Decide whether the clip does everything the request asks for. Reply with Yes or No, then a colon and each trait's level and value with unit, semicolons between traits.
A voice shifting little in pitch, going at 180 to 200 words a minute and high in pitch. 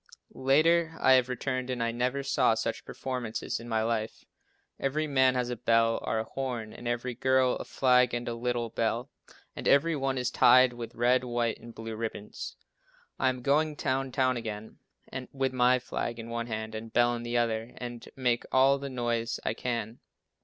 No: narrow, 2.1 semitones; average, 195 wpm; low, 125 Hz